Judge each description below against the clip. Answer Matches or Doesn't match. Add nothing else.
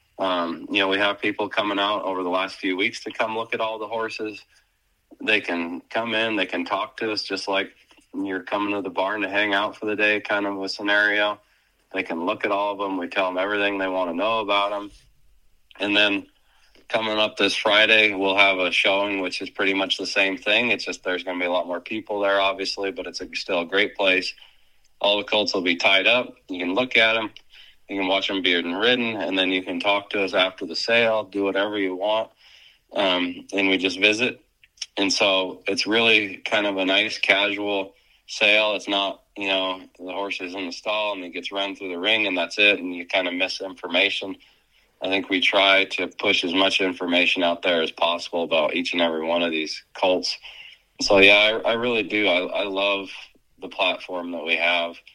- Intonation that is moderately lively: Doesn't match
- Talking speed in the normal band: Doesn't match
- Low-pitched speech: Matches